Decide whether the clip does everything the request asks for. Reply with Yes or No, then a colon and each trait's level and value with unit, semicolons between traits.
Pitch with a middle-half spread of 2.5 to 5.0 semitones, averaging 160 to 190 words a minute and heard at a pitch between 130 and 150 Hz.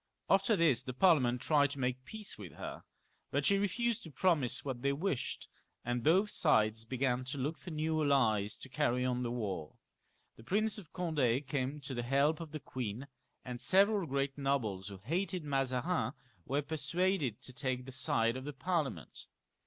Yes: average, 4.5 semitones; average, 185 wpm; medium, 140 Hz